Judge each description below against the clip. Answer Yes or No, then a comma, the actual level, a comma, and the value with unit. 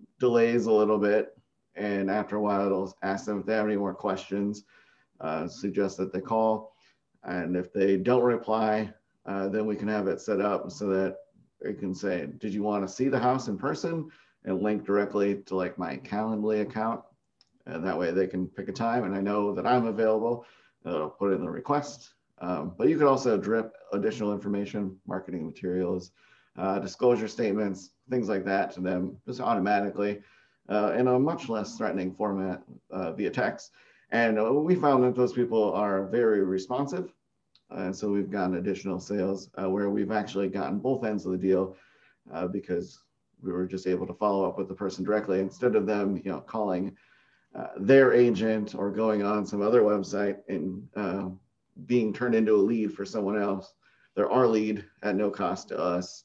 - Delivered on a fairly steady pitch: Yes, narrow, 2.3 semitones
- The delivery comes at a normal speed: Yes, average, 190 wpm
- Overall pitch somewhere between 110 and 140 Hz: No, low, 100 Hz